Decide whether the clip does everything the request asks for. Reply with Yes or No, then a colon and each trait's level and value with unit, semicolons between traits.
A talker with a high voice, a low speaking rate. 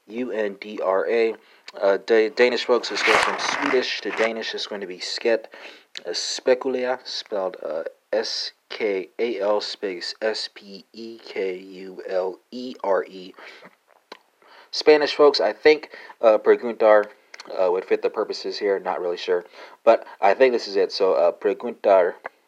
Yes: very high, 395 Hz; slow, 120 wpm